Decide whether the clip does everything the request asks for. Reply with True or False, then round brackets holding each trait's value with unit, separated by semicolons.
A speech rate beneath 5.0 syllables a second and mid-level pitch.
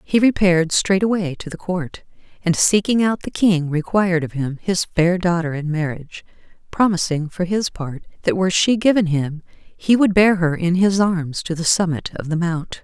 True (4.8 syllables/s; 175 Hz)